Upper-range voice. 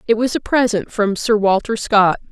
Yes: high, 210 Hz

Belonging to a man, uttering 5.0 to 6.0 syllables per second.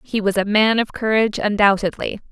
No: female; 5.7 syllables/s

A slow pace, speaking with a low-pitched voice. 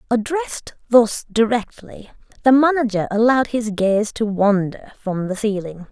No: slow, 130 wpm; high, 220 Hz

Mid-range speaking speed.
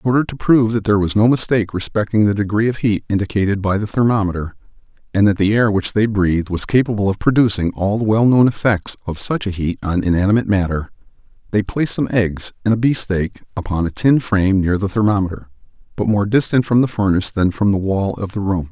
No: fast, 220 wpm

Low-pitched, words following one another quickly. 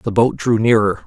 Yes: low, 110 Hz; fast, 225 wpm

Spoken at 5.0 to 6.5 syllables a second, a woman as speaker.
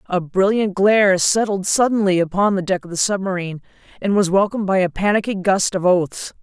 Yes: 5.6 syllables/s; female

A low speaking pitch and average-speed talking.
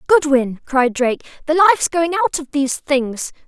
No: very high, 290 Hz; average, 175 wpm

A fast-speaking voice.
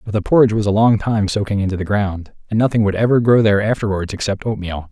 Yes: fast, 245 wpm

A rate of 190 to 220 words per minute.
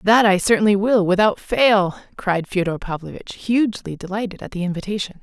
No: average, 160 wpm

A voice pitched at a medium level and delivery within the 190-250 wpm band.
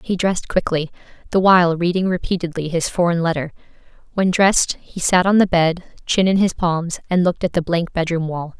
Yes: medium, 175 Hz; average, 195 wpm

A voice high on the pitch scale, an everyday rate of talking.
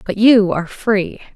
Yes: high, 200 Hz; average, 175 wpm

